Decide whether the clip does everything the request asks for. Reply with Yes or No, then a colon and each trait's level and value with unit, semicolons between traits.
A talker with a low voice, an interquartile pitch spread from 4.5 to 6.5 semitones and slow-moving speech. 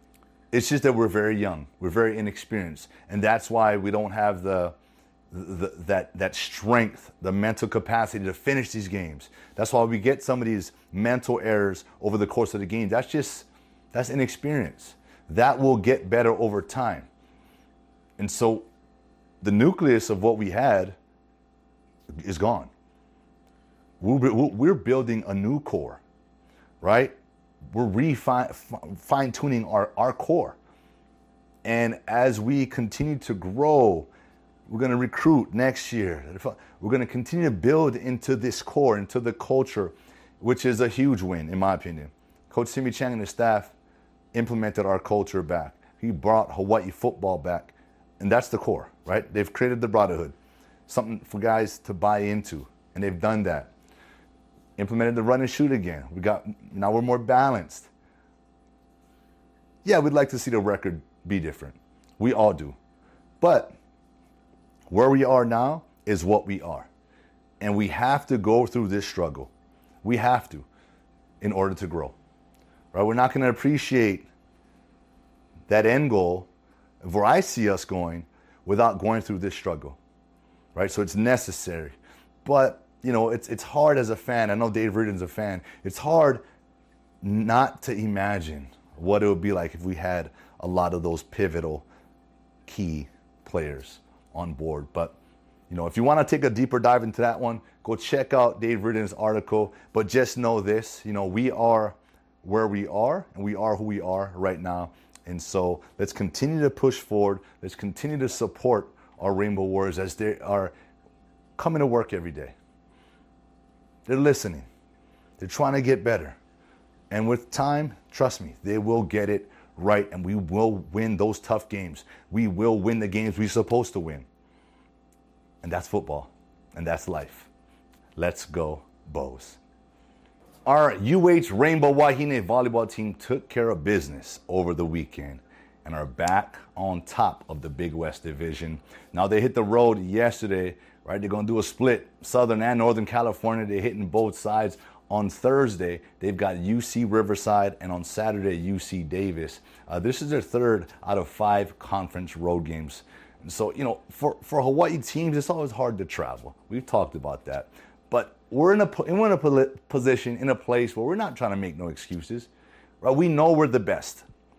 No: low, 105 Hz; average, 5.3 semitones; average, 170 wpm